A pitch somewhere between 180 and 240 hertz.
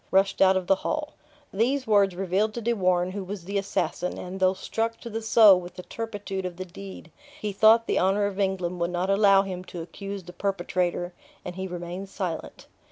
Yes: high, 190 Hz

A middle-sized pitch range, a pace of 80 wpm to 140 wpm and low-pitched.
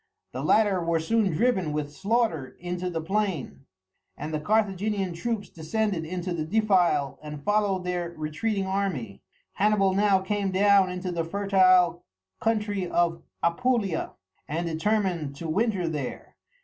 No: average, 3.9 semitones; slow, 135 wpm; medium, 185 Hz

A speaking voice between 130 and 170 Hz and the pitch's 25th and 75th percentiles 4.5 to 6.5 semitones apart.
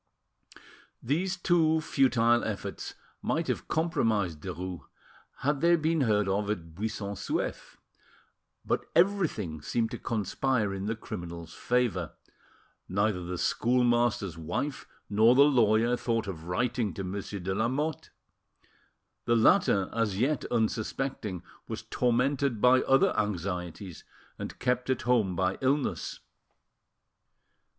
No: low, 115 Hz; average, 5.2 semitones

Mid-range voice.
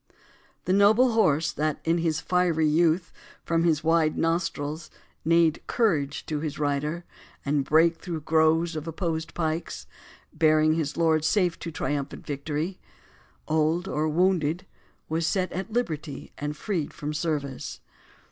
Yes: medium, 160 Hz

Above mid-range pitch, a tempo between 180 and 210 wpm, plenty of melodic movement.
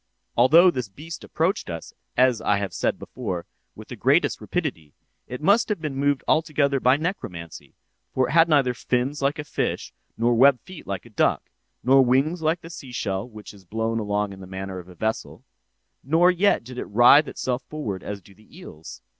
No: low, 125 Hz; average, 190 wpm; wide, 6.9 semitones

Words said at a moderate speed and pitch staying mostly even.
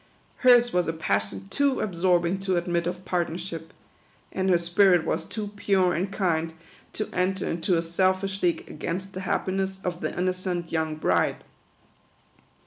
Yes: average, 150 wpm; narrow, 2.2 semitones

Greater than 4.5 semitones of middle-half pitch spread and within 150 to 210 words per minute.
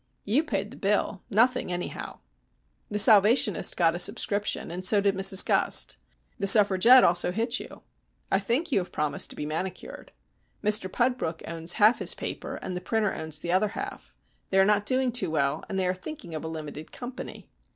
No: average, 3.9 semitones; average, 190 wpm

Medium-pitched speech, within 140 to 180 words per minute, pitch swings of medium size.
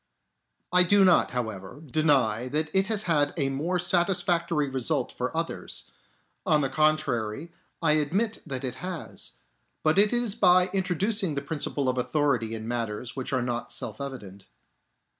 No: medium, 150 Hz; average, 155 wpm; wide, 5.9 semitones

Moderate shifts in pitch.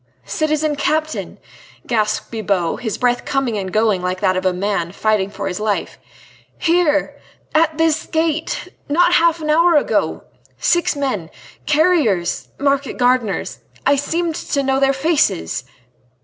No: wide, 7.2 semitones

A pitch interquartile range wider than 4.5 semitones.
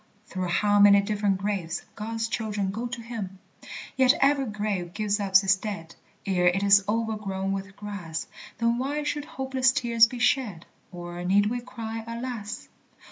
No: average, 3.3 semitones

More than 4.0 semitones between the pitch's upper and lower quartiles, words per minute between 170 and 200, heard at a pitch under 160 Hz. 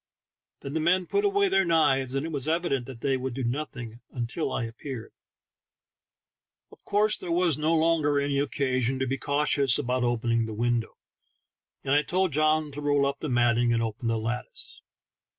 Yes: average, 4.4 semitones; average, 185 wpm; medium, 140 Hz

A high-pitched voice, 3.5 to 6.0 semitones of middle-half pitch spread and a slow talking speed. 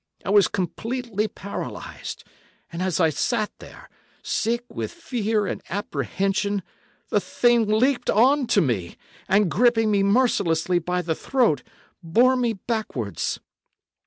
Yes: high, 210 Hz; average, 4.7 semitones; slow, 130 wpm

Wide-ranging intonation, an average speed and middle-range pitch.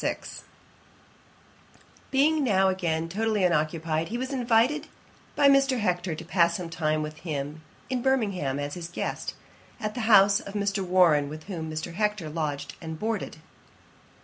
Yes: wide, 5.7 semitones; average, 150 wpm; medium, 180 Hz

